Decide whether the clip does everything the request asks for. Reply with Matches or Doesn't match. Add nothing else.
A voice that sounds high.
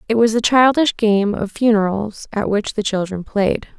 Matches